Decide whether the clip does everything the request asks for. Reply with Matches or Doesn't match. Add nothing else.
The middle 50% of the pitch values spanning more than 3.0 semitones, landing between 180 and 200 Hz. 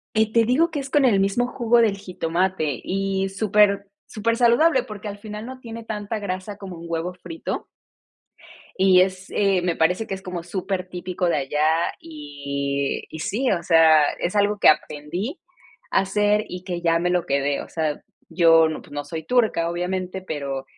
Matches